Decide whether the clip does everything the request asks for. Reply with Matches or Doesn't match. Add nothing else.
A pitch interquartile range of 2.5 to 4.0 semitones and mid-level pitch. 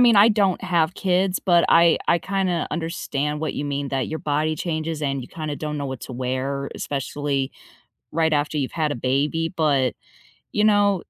Matches